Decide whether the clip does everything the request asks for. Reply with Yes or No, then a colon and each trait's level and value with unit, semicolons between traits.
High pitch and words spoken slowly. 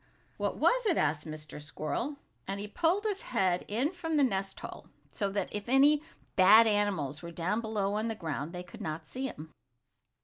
No: high, 205 Hz; average, 195 wpm